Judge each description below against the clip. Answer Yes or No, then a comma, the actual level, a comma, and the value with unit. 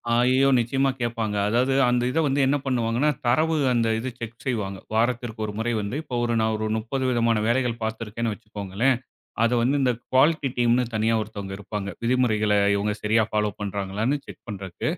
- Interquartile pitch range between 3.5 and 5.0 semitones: No, average, 2.9 semitones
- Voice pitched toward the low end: Yes, low, 115 Hz